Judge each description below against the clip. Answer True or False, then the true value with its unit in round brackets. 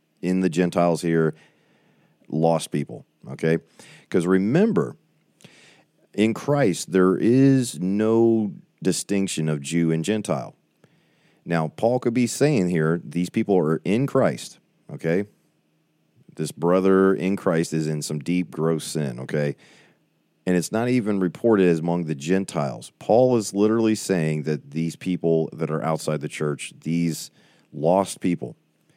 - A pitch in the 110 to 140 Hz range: False (85 Hz)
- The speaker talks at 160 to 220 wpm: False (135 wpm)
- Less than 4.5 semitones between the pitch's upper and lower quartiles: True (3.9 semitones)